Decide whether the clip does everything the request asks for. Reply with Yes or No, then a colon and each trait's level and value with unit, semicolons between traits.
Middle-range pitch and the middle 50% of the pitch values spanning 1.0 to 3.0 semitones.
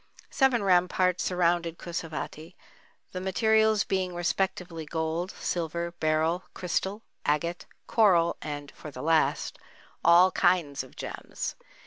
Yes: medium, 175 Hz; narrow, 2.5 semitones